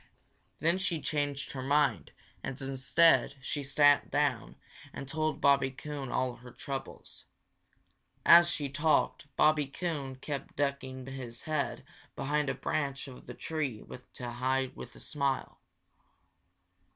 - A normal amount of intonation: No, narrow, 2.3 semitones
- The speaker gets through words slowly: Yes, slow, 125 wpm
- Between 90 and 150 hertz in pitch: Yes, medium, 140 Hz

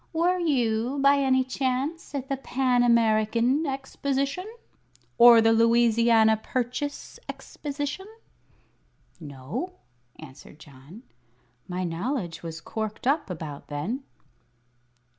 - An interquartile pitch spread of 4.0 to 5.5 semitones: Yes, average, 4.3 semitones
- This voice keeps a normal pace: No, slow, 100 wpm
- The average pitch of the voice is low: No, high, 240 Hz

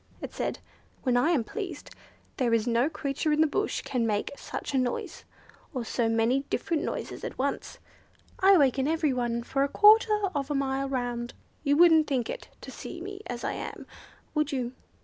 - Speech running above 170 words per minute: Yes, average, 190 wpm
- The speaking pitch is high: Yes, very high, 275 Hz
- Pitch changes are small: No, average, 4.5 semitones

